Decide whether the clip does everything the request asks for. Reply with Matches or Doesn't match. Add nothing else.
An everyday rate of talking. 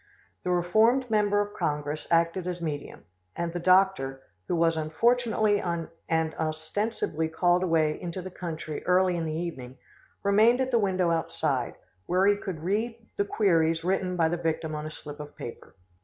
Matches